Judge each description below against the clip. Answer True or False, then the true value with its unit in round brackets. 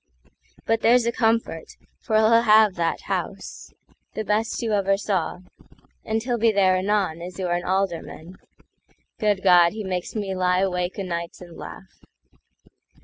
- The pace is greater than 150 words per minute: False (140 wpm)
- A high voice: True (195 Hz)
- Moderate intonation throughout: True (3.3 semitones)